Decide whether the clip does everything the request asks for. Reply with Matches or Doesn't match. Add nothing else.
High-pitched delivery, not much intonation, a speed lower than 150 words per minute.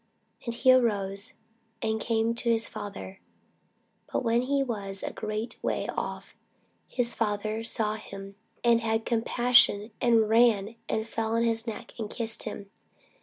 Doesn't match